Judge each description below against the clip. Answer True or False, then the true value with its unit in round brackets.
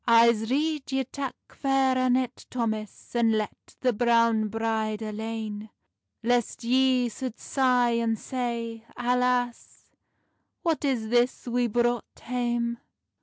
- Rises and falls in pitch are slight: True (2.0 semitones)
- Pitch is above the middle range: True (240 Hz)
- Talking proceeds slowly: True (120 wpm)